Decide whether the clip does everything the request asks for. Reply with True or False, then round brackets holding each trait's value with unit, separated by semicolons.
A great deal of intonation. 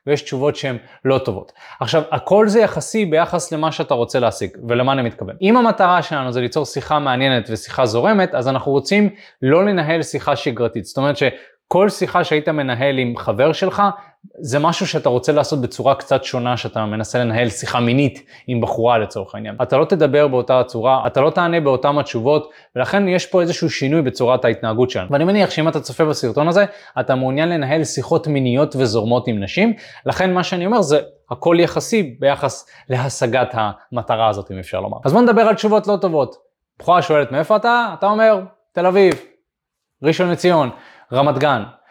True (5.9 semitones)